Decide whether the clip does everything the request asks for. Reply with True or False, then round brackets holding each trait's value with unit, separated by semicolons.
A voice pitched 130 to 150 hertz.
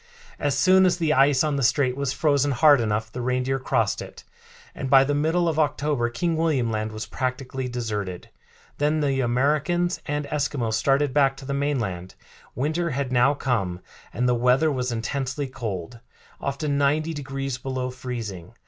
True (135 Hz)